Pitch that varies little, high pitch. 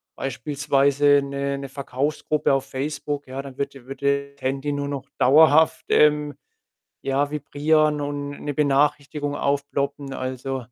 No: narrow, 1.2 semitones; medium, 140 Hz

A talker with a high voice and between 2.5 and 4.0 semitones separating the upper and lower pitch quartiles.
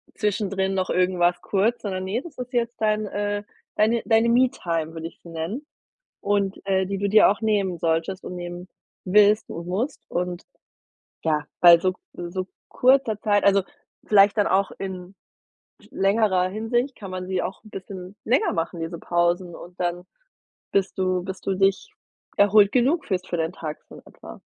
Yes: high, 195 Hz; average, 2.9 semitones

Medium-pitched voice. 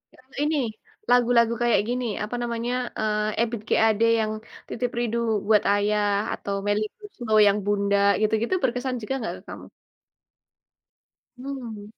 No: high, 230 Hz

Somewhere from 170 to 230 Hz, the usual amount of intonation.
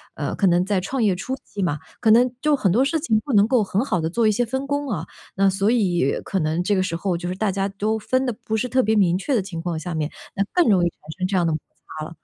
Yes: high, 200 Hz; average, 4.9 semitones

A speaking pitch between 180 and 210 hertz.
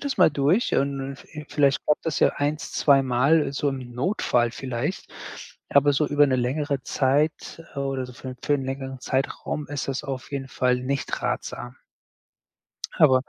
No: low, 135 Hz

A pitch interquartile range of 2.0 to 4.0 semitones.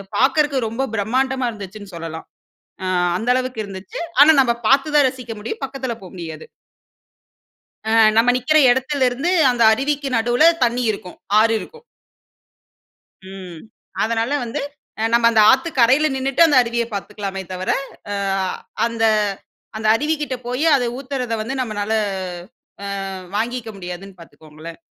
No: average, 4.7 semitones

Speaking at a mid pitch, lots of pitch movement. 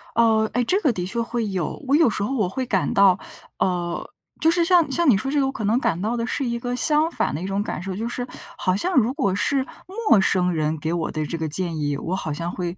No: high, 215 Hz; wide, 6.3 semitones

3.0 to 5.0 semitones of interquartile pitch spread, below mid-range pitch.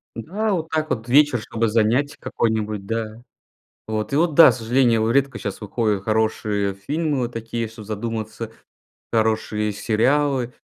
Yes: average, 4.0 semitones; low, 115 Hz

